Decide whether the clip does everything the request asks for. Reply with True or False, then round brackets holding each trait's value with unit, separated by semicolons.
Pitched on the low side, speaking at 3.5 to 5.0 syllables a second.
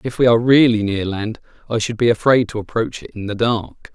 False (115 Hz; 5.6 syllables/s)